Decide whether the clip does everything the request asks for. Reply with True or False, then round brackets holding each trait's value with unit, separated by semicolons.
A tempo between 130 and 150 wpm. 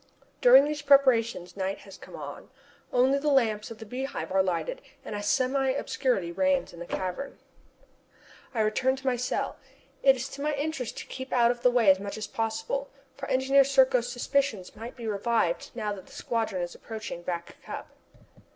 False (190 wpm)